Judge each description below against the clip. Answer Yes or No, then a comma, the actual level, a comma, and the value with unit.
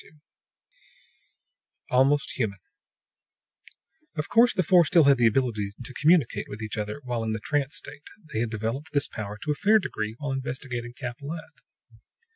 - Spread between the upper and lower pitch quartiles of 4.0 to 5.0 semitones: Yes, average, 4.7 semitones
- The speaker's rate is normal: Yes, average, 160 wpm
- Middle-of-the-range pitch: No, low, 130 Hz